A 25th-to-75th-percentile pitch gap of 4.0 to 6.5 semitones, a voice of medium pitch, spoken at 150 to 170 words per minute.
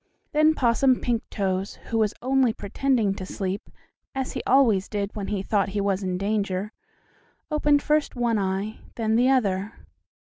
No: average, 4.5 semitones; high, 215 Hz; average, 160 wpm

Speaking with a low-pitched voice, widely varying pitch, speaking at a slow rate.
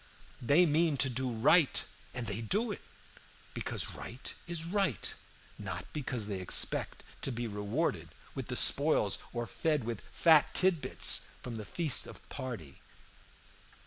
No: low, 130 Hz; wide, 6.2 semitones; average, 145 wpm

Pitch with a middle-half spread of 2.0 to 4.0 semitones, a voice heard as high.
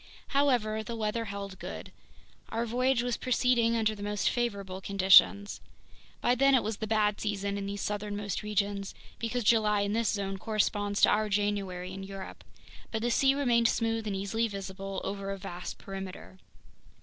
Yes: narrow, 2.5 semitones; high, 210 Hz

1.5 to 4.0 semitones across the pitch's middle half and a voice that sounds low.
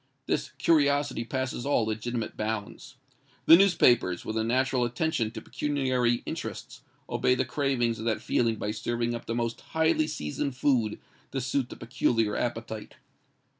Yes: average, 3.3 semitones; low, 120 Hz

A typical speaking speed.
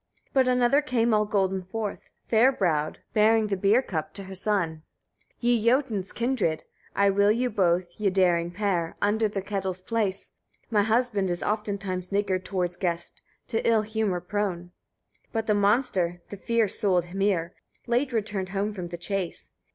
Yes: average, 170 wpm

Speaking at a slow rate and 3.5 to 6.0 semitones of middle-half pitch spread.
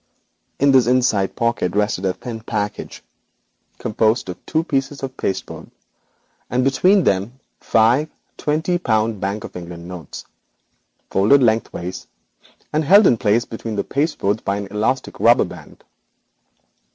Yes: slow, 125 wpm; average, 5.0 semitones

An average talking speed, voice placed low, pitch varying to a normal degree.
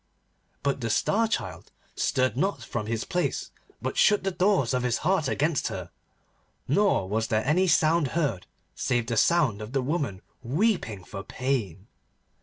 No: average, 160 wpm; low, 130 Hz; wide, 7.4 semitones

